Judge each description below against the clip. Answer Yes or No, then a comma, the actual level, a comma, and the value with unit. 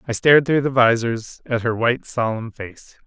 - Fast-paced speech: No, average, 195 wpm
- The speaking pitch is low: Yes, low, 120 Hz